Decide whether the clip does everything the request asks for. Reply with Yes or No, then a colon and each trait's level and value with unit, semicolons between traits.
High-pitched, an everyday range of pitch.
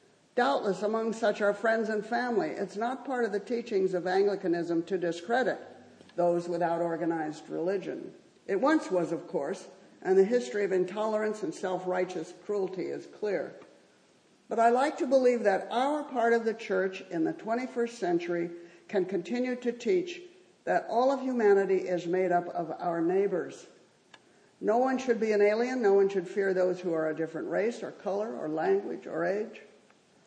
Yes: high, 200 Hz; average, 4.9 semitones